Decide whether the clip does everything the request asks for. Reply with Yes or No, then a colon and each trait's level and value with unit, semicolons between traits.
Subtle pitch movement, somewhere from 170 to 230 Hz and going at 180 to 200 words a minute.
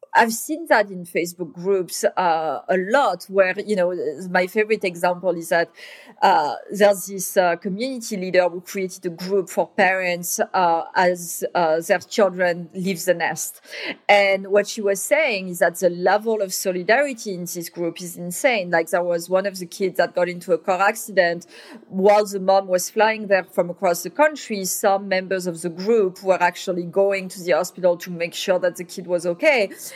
Yes: narrow, 2.3 semitones; medium, 185 Hz; average, 190 wpm